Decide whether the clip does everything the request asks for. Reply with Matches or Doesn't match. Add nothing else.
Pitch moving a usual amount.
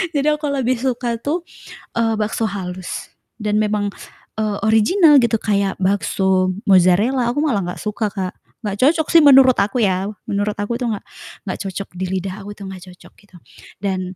Matches